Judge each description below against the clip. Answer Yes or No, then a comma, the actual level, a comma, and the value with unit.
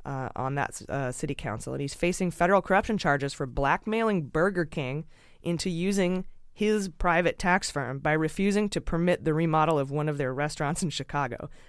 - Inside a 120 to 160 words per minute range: No, average, 180 wpm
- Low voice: No, medium, 155 Hz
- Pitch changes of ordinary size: Yes, average, 4.3 semitones